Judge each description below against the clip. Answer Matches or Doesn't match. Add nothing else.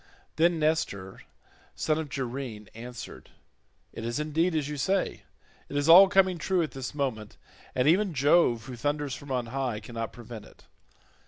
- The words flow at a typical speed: Matches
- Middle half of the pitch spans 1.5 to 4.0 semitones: Doesn't match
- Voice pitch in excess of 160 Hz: Doesn't match